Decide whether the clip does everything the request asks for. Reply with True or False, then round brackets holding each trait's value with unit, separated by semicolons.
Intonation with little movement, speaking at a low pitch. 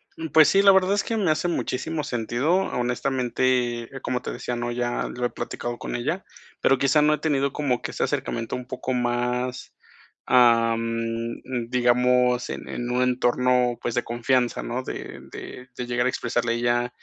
True (1.9 semitones; 125 Hz)